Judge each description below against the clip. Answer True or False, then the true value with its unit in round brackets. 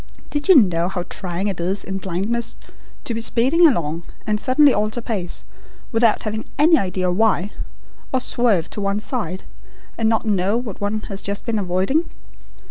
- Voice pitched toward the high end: True (210 Hz)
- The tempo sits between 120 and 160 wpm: False (170 wpm)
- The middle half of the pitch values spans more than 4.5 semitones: False (4.0 semitones)